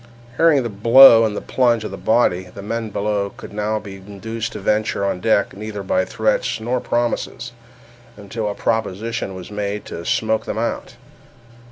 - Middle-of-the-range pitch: No, low, 105 Hz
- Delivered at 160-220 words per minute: Yes, average, 175 wpm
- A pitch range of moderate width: No, narrow, 2.3 semitones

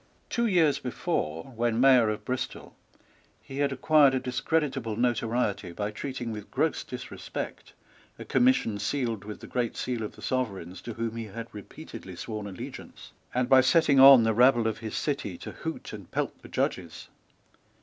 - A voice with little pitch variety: No, average, 3.8 semitones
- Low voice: Yes, low, 120 Hz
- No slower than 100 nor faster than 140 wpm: No, average, 170 wpm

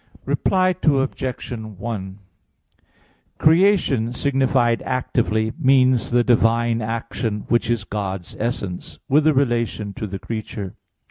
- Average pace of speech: No, slow, 110 wpm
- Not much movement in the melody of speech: No, average, 3.6 semitones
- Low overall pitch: Yes, low, 120 Hz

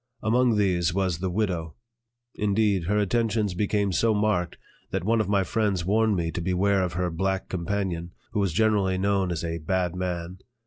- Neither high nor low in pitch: No, very low, 95 Hz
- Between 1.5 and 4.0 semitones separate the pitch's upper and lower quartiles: Yes, average, 2.9 semitones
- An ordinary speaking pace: Yes, average, 180 wpm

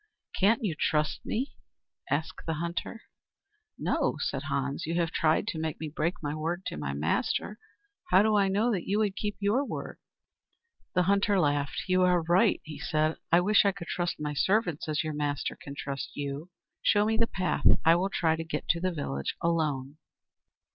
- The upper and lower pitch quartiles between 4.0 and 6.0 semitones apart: Yes, average, 4.6 semitones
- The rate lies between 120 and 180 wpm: No, average, 190 wpm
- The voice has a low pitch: No, medium, 170 Hz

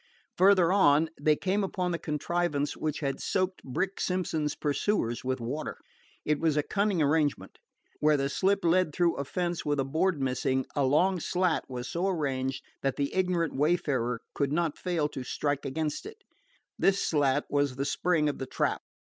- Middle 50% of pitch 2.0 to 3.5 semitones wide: No, average, 4.2 semitones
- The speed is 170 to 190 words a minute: Yes, average, 175 wpm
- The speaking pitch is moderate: Yes, medium, 150 Hz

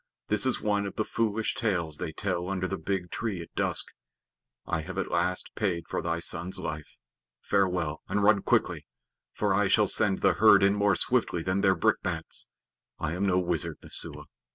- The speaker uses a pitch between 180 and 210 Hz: No, very low, 95 Hz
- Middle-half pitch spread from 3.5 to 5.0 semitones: No, average, 2.9 semitones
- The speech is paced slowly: No, average, 185 wpm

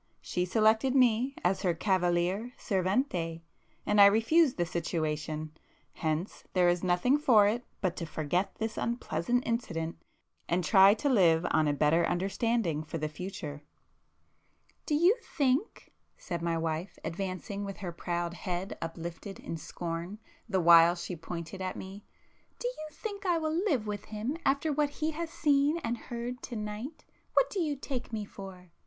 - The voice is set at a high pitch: Yes, high, 195 Hz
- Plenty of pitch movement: Yes, wide, 6.4 semitones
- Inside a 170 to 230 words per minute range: No, average, 155 wpm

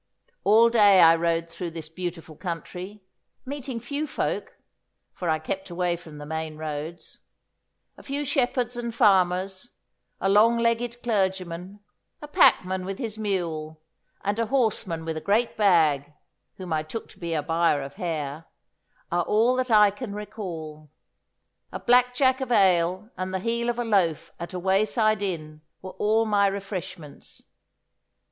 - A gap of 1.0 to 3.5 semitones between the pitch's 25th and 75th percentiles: No, average, 5.3 semitones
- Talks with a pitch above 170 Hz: Yes, high, 190 Hz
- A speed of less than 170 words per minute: Yes, average, 155 wpm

